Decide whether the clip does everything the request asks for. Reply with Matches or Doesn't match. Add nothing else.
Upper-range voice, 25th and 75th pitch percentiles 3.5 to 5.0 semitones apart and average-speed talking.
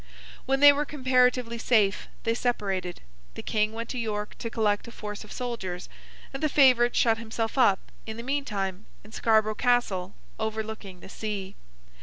Doesn't match